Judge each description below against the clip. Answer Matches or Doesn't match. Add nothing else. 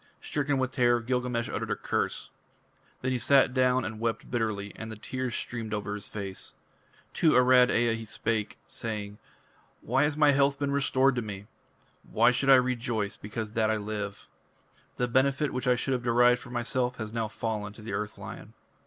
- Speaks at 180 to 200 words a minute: Matches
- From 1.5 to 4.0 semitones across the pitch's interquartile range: Matches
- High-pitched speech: Doesn't match